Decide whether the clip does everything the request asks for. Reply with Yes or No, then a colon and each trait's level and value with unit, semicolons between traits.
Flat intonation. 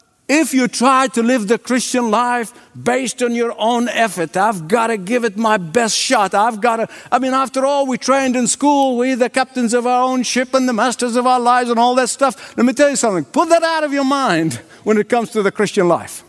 Yes: narrow, 2.2 semitones